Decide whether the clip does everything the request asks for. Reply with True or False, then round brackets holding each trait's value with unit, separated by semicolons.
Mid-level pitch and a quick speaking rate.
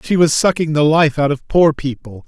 True (150 Hz; 240 wpm)